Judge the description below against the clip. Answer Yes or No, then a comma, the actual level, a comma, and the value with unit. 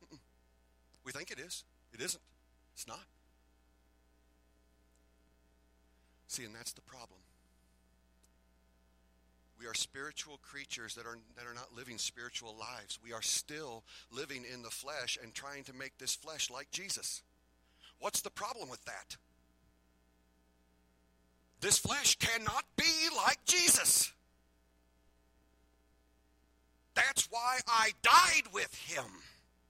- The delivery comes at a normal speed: No, slow, 115 wpm